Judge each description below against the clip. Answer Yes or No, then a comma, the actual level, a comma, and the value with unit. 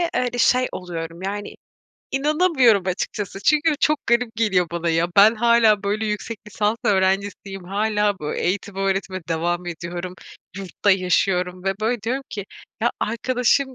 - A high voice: Yes, high, 205 Hz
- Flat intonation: No, average, 4.2 semitones